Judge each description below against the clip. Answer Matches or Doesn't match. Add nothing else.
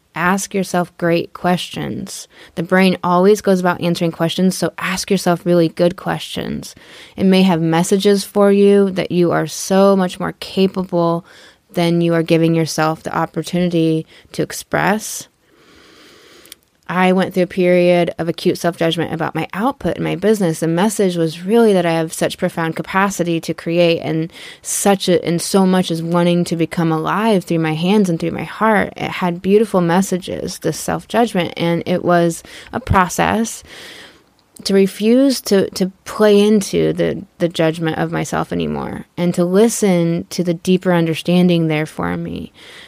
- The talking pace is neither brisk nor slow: Matches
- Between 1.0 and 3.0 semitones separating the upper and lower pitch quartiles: Matches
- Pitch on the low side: Doesn't match